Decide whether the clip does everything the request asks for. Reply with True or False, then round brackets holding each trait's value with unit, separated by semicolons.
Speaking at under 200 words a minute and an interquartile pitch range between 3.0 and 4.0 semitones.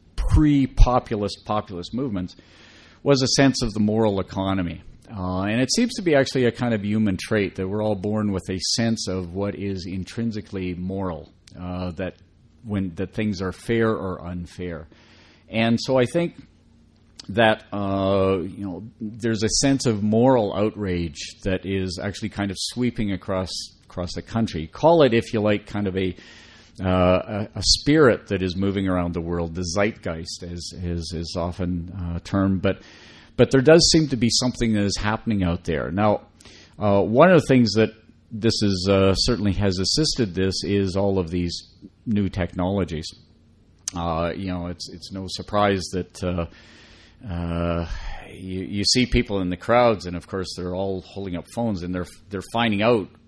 True (175 wpm; 3.6 semitones)